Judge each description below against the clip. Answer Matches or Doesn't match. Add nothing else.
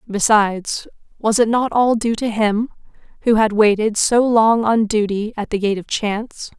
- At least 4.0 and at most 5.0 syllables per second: Matches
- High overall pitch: Matches